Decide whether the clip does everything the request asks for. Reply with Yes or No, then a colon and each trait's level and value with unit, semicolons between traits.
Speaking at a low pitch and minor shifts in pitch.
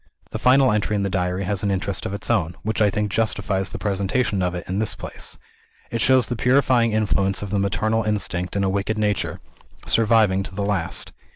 Yes: low, 100 Hz; narrow, 2.3 semitones